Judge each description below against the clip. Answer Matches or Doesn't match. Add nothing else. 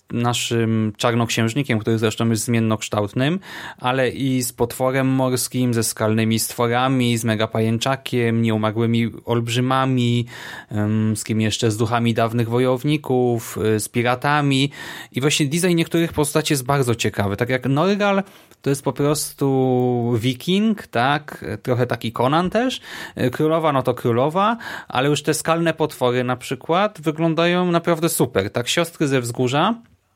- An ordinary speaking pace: Matches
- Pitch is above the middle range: Doesn't match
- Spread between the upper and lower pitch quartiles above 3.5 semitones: Matches